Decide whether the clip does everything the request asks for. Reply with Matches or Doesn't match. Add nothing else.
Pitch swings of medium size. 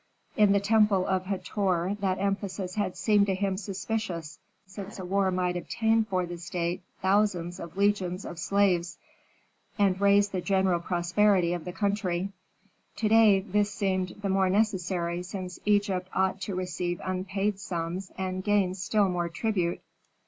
Doesn't match